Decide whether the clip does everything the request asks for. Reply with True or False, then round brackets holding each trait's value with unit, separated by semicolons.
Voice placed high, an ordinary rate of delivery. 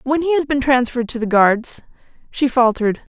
True (255 Hz; 190 wpm)